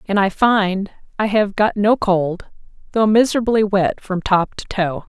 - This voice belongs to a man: No, female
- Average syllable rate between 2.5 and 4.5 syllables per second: Yes, 4.3 syllables/s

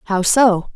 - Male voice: No, female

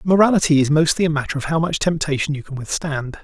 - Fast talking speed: Yes, fast, 220 wpm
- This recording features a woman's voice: No, male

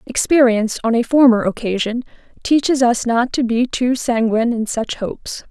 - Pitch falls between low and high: No, high, 240 Hz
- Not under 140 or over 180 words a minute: Yes, average, 165 wpm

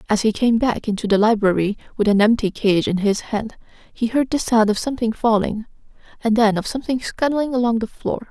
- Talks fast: Yes, fast, 210 wpm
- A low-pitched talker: No, high, 225 Hz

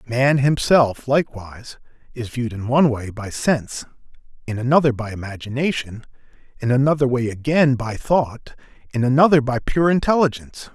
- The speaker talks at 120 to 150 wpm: Yes, average, 140 wpm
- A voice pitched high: No, low, 130 Hz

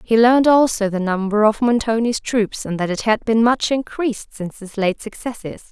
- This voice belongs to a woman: Yes, female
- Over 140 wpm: Yes, average, 200 wpm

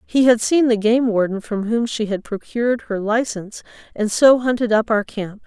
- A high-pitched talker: Yes, high, 225 Hz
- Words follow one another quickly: Yes, fast, 210 wpm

